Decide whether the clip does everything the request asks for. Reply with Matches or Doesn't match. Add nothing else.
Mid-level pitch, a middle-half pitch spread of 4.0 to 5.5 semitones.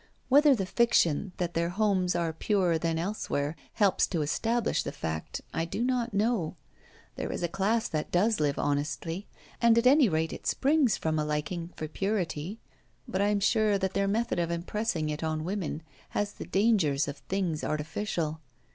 Matches